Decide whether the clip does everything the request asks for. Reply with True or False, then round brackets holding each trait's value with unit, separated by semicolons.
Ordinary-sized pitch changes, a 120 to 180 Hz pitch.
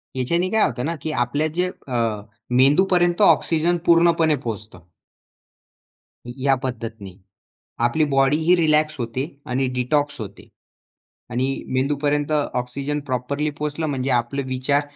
True (3.9 semitones; 140 Hz)